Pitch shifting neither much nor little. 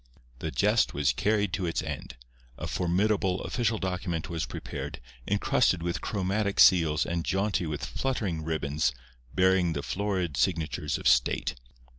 Yes: average, 3.9 semitones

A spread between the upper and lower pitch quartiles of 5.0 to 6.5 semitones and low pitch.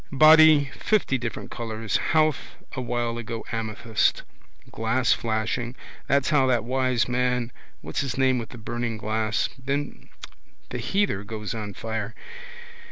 No: average, 2.8 semitones; low, 120 Hz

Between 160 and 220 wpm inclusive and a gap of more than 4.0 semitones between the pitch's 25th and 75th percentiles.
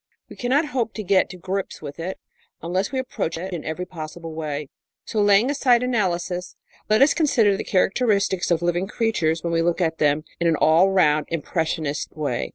Yes: average, 190 wpm; average, 4.5 semitones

